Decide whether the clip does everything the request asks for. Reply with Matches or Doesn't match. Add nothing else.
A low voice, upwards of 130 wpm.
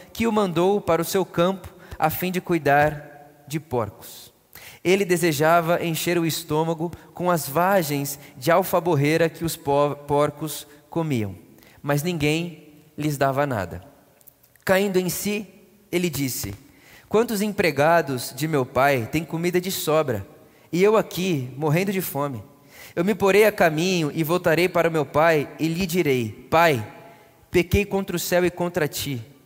Doesn't match